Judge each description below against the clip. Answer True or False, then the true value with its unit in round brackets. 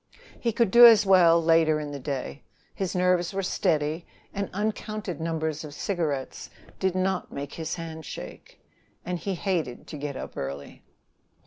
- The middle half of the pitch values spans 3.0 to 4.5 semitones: True (4.0 semitones)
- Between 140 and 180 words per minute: True (160 wpm)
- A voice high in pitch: False (165 Hz)